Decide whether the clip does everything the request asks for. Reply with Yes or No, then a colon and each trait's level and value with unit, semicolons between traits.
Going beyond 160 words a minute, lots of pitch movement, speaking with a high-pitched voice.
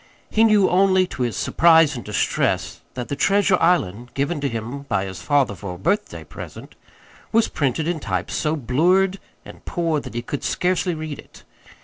No: average, 185 wpm; wide, 7.1 semitones; medium, 150 Hz